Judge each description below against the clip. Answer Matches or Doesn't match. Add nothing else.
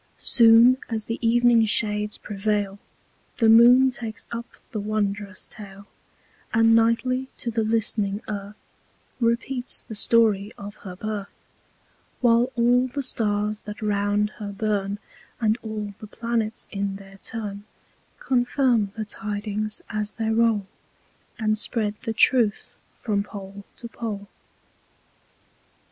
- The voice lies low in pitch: Doesn't match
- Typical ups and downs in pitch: Doesn't match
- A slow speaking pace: Matches